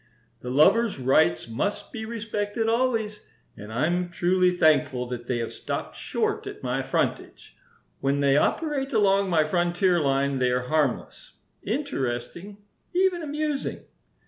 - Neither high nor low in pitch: Yes, medium, 175 Hz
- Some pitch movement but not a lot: No, wide, 8.5 semitones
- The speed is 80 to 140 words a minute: Yes, slow, 135 wpm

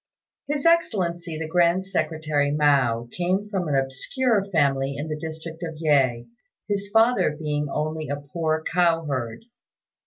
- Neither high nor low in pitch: Yes, medium, 160 Hz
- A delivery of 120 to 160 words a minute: Yes, average, 145 wpm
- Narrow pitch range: No, average, 3.8 semitones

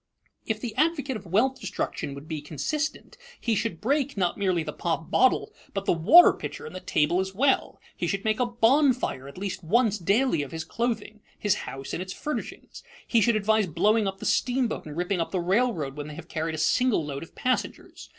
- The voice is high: Yes, high, 200 Hz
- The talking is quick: Yes, fast, 210 wpm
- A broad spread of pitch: Yes, wide, 6.6 semitones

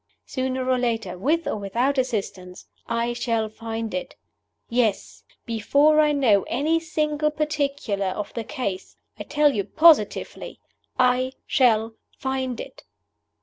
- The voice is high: Yes, very high, 250 Hz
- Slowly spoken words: Yes, slow, 130 wpm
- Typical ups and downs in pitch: Yes, average, 4.7 semitones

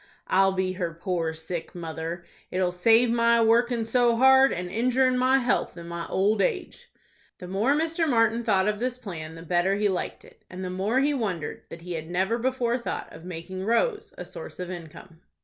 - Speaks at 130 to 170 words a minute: No, average, 200 wpm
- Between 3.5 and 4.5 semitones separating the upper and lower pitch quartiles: No, wide, 5.4 semitones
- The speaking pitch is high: Yes, high, 195 Hz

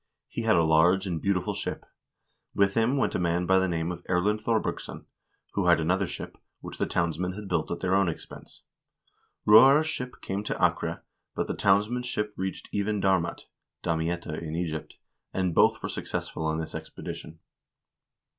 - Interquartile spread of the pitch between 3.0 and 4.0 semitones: Yes, average, 3.5 semitones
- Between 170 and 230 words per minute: Yes, average, 175 wpm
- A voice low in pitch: Yes, very low, 95 Hz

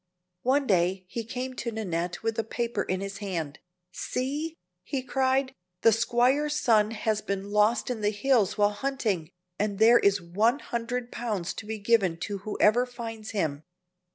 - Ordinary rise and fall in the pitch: Yes, average, 3.7 semitones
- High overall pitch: Yes, high, 220 Hz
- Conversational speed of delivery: Yes, average, 165 wpm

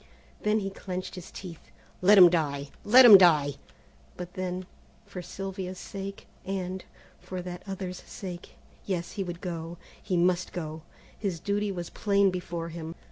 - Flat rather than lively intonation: Yes, narrow, 2.0 semitones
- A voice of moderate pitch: Yes, medium, 180 Hz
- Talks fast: No, average, 155 wpm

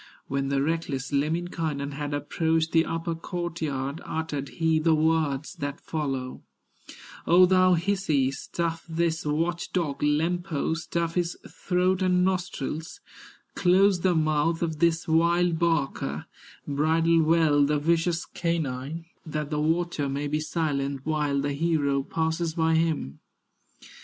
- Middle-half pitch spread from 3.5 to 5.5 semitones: No, average, 2.7 semitones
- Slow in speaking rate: Yes, slow, 130 wpm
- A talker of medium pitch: Yes, medium, 160 Hz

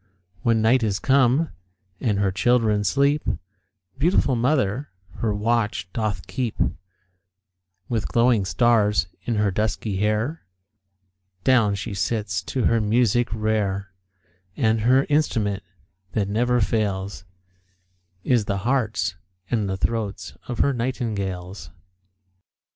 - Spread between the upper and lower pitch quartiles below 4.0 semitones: Yes, average, 3.4 semitones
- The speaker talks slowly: Yes, slow, 115 wpm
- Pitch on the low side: Yes, low, 110 Hz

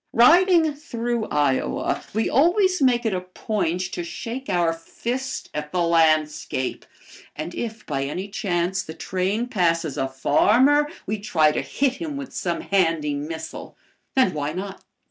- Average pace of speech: Yes, average, 150 wpm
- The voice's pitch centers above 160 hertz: Yes, high, 190 Hz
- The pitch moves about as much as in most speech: No, wide, 7.3 semitones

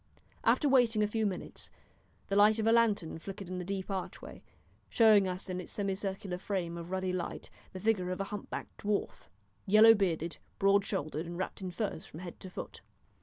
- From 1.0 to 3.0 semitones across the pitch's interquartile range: Yes, narrow, 2.5 semitones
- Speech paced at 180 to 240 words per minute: Yes, average, 190 wpm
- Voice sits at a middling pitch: No, high, 195 Hz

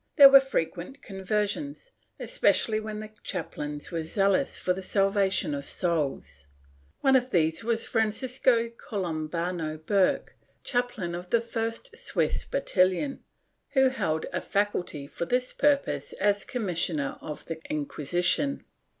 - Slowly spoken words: Yes, slow, 125 wpm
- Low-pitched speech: No, high, 195 Hz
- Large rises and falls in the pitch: Yes, wide, 6.5 semitones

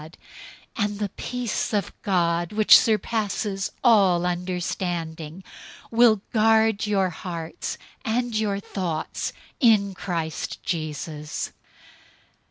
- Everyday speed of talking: No, slow, 95 wpm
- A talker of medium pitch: No, high, 195 Hz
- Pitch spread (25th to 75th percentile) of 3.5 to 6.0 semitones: Yes, average, 4.0 semitones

